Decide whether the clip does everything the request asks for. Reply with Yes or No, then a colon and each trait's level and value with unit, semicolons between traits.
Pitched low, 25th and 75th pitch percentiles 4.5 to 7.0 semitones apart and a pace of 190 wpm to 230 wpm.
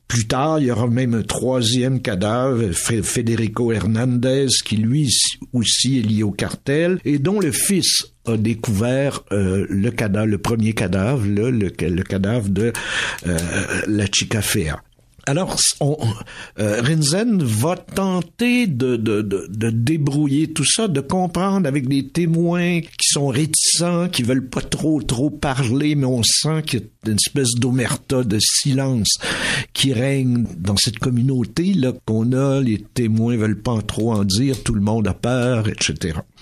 No: low, 125 Hz; average, 4.9 semitones; average, 160 wpm